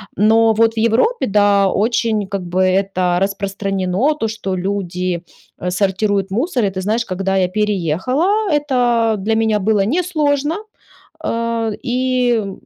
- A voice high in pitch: Yes, high, 210 Hz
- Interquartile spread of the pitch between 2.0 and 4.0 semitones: Yes, average, 3.3 semitones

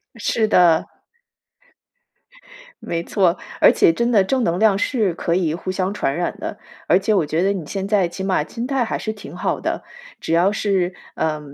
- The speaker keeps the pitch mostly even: No, average, 3.7 semitones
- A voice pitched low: No, high, 190 Hz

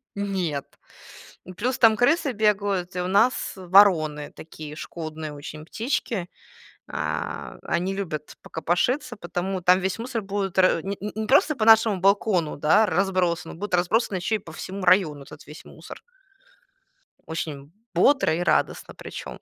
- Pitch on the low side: No, medium, 185 Hz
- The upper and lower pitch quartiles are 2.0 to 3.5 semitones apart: No, average, 4.1 semitones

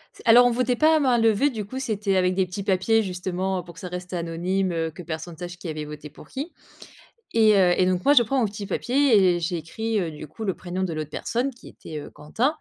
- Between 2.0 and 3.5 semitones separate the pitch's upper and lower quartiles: No, average, 4.7 semitones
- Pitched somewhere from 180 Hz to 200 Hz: Yes, high, 190 Hz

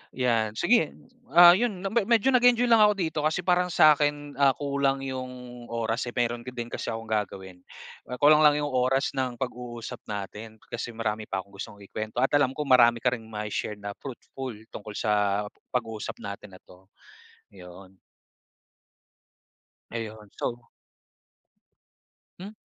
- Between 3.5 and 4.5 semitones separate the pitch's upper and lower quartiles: No, average, 5.2 semitones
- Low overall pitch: Yes, low, 120 Hz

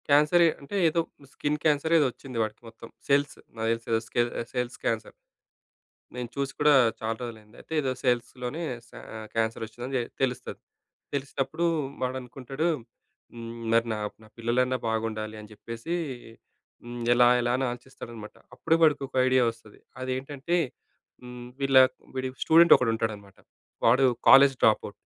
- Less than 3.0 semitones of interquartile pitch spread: No, average, 3.4 semitones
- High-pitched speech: No, low, 125 Hz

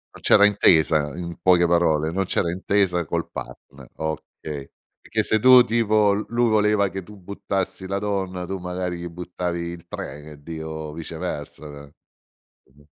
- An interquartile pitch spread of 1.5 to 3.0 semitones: No, average, 4.0 semitones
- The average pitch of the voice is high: No, very low, 90 Hz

